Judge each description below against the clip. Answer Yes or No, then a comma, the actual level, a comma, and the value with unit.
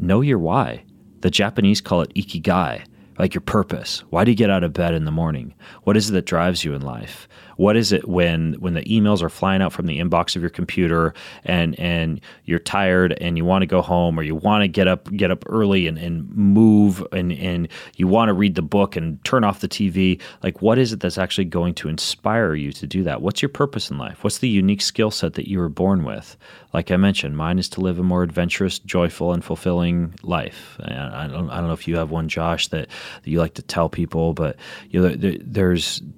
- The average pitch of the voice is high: No, very low, 90 Hz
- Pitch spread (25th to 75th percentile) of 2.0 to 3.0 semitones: Yes, average, 2.7 semitones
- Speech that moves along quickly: Yes, fast, 240 wpm